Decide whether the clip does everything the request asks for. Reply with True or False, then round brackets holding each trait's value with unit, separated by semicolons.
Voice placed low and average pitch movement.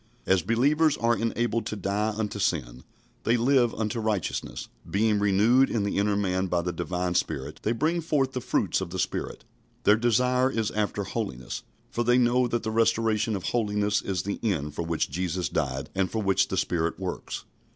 True (105 Hz; 4.2 semitones)